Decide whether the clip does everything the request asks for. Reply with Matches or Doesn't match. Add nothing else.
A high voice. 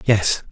Doesn't match